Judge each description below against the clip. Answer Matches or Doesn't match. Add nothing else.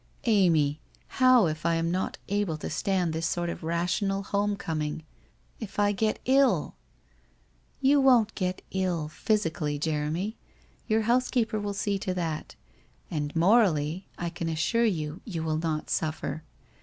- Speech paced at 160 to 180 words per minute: Matches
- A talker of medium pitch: Matches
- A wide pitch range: Doesn't match